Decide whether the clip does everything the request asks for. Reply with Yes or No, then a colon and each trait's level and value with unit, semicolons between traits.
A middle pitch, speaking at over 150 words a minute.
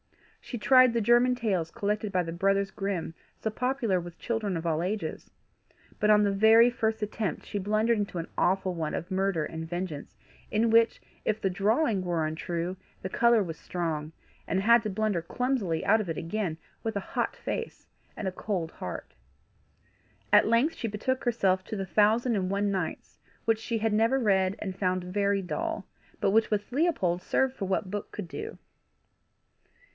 No: high, 200 Hz; average, 180 wpm